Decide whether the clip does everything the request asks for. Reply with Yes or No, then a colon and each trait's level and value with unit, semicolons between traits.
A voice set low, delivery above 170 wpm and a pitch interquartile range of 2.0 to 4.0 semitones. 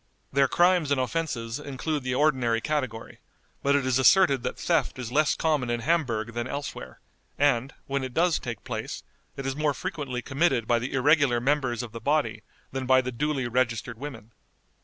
Yes: low, 130 Hz; average, 180 wpm; average, 3.6 semitones